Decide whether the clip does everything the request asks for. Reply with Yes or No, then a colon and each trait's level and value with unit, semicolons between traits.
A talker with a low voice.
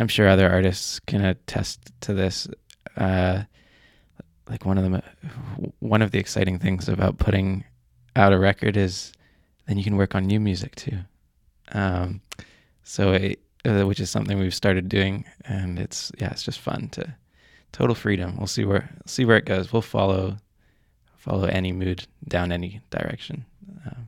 Yes: very low, 95 Hz